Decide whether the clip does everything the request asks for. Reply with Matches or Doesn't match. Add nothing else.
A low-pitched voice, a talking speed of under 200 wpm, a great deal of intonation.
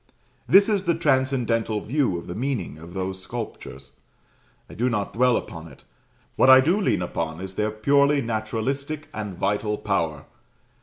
Matches